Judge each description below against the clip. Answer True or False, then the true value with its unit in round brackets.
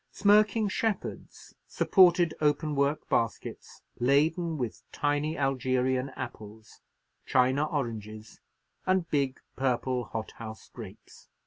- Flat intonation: False (4.5 semitones)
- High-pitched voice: False (140 Hz)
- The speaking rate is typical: False (95 wpm)